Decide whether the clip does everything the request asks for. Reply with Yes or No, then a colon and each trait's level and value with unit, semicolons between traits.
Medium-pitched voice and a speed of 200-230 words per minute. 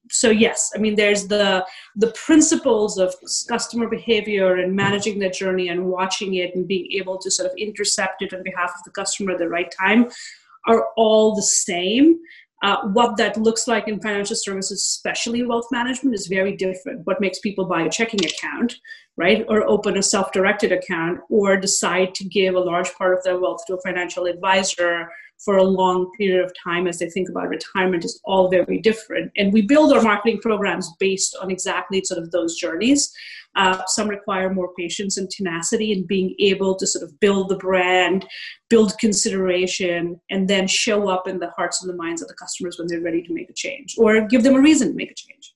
No: high, 195 Hz; fast, 205 wpm